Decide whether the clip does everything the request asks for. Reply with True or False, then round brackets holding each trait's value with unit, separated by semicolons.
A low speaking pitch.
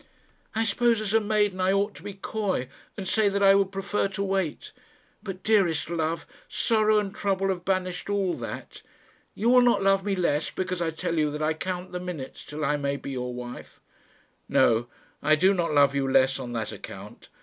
False (185 Hz)